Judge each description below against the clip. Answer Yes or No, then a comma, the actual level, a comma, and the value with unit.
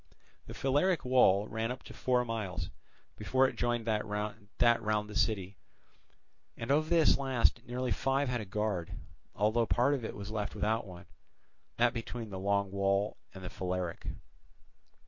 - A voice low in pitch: Yes, low, 110 Hz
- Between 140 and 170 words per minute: Yes, average, 160 wpm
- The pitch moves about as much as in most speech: Yes, average, 3.6 semitones